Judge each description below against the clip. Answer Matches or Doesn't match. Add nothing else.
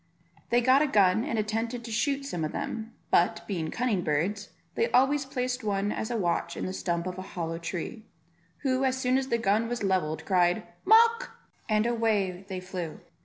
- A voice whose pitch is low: Doesn't match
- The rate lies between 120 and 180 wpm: Doesn't match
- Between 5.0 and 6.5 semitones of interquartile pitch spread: Matches